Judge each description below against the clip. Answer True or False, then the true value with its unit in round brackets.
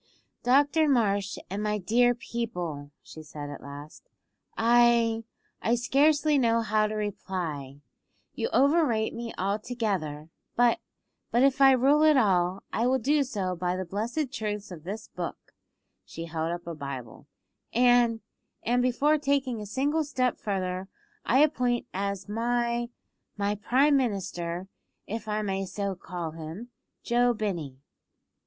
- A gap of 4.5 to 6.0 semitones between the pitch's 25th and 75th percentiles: True (5.1 semitones)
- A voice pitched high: True (220 Hz)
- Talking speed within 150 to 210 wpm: False (140 wpm)